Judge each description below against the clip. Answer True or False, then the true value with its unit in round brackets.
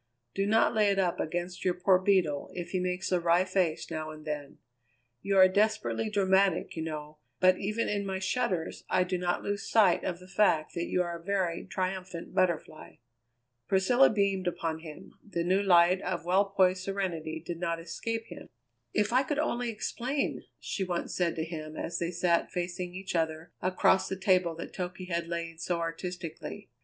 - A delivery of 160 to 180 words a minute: False (190 wpm)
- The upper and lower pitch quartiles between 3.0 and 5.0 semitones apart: False (2.5 semitones)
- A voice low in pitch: False (180 Hz)